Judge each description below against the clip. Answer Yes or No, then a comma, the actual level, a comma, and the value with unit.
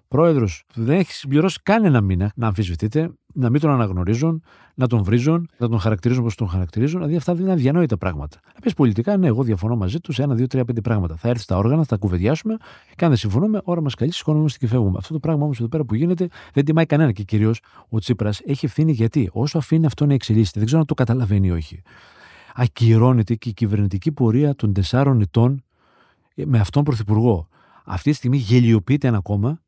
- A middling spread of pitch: No, wide, 5.7 semitones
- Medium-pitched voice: No, low, 125 Hz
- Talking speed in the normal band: No, fast, 210 wpm